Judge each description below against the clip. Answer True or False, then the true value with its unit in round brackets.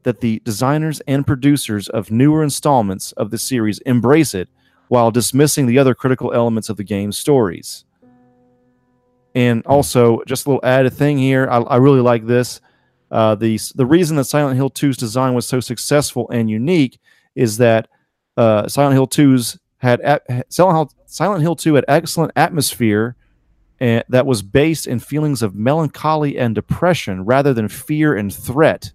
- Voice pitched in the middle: False (125 Hz)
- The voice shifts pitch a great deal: False (3.5 semitones)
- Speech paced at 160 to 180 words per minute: True (170 wpm)